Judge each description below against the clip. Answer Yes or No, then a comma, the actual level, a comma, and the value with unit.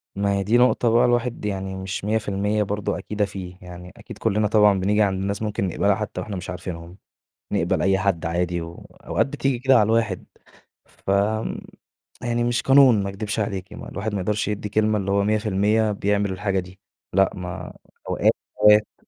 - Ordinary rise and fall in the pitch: No, narrow, 2.1 semitones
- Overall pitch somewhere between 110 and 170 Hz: No, low, 100 Hz